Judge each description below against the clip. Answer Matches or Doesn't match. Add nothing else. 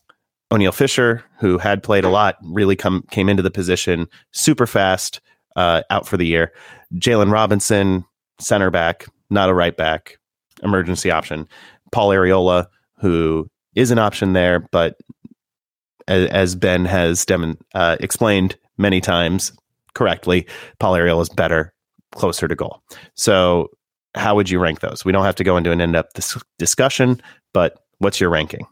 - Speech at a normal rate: Matches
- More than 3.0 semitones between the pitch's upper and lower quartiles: Doesn't match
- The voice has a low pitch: Matches